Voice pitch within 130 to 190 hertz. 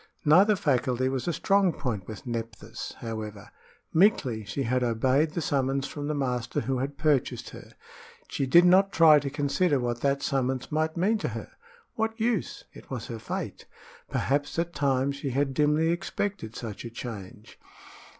Yes: medium, 140 Hz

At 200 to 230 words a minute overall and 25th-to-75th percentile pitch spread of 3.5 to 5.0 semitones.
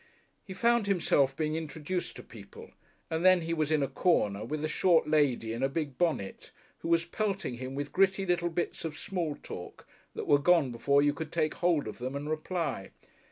Yes: fast, 205 wpm; average, 3.9 semitones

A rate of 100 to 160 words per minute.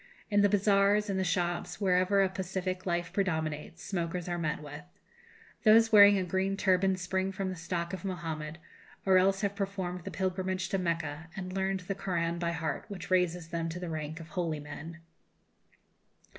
No: average, 180 wpm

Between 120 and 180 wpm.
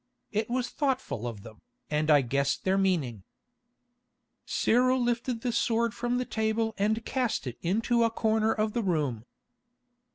Yes: average, 155 wpm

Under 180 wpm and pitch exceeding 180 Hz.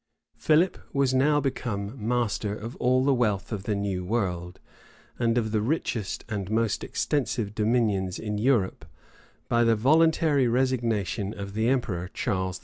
No: average, 150 wpm; low, 115 Hz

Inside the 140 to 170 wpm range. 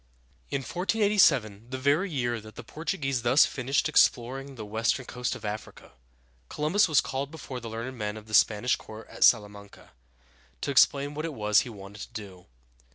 No: average, 185 wpm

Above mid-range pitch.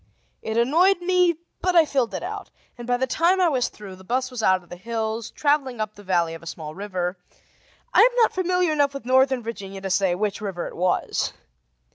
Yes: high, 235 Hz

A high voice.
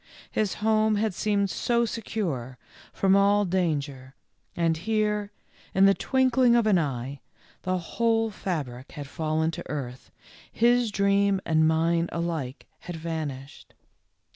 No: medium, 180 Hz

